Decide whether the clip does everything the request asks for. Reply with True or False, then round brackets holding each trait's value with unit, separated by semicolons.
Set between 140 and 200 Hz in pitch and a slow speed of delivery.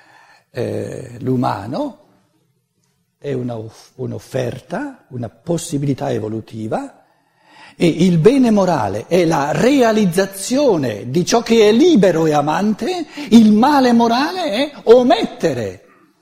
True (185 Hz; 100 wpm)